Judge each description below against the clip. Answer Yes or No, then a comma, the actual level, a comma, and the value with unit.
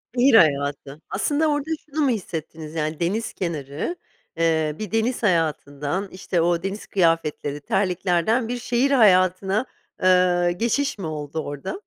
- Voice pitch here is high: No, medium, 180 Hz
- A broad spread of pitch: Yes, wide, 6.1 semitones